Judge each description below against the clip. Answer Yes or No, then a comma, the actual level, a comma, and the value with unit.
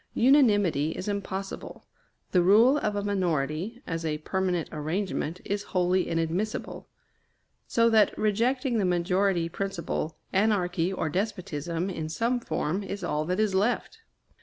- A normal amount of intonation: Yes, average, 3.8 semitones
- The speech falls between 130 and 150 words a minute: Yes, slow, 135 wpm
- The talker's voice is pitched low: No, high, 190 Hz